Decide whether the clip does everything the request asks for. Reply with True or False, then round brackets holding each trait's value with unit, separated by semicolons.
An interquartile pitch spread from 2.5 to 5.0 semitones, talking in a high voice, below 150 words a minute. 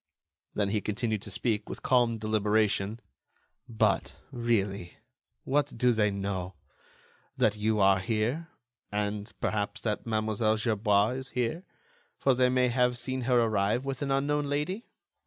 False (3.4 semitones; 110 Hz; 140 wpm)